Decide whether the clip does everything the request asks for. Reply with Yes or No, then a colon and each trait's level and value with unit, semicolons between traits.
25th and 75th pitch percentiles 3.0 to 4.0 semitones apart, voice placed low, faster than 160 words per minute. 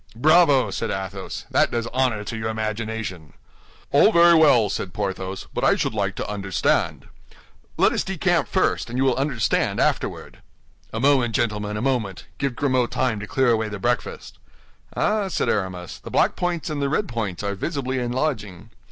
No: average, 4.6 semitones; low, 115 Hz; average, 180 wpm